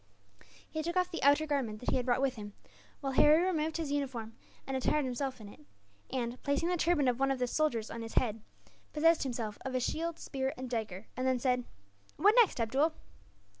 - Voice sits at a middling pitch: No, very high, 265 Hz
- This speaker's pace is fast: Yes, fast, 210 wpm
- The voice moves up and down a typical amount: Yes, average, 4.2 semitones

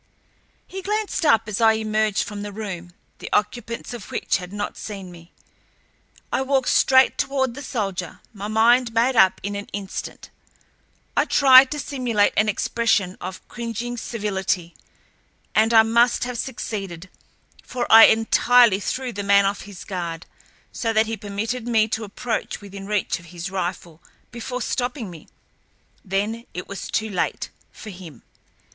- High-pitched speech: Yes, high, 215 Hz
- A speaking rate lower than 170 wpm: Yes, average, 155 wpm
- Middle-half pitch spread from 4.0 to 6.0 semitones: No, average, 3.5 semitones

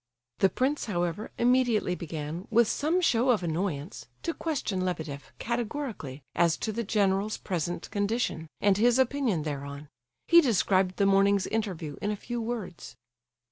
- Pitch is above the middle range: Yes, high, 200 Hz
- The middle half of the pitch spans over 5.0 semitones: Yes, wide, 5.6 semitones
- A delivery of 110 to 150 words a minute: Yes, average, 145 wpm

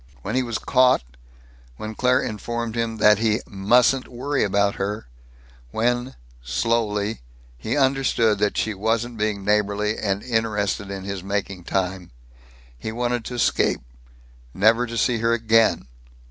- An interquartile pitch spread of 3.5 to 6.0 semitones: No, narrow, 2.6 semitones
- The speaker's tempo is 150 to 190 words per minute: No, average, 140 wpm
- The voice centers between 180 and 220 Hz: No, low, 110 Hz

